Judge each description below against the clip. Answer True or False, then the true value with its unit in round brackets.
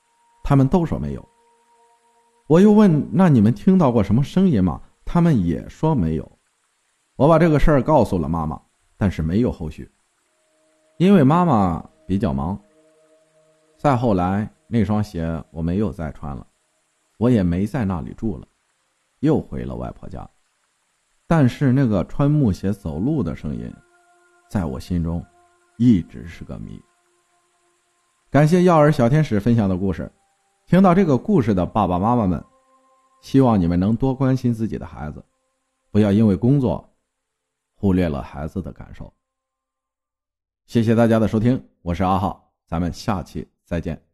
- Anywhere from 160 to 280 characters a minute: True (225 characters per minute)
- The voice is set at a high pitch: False (120 Hz)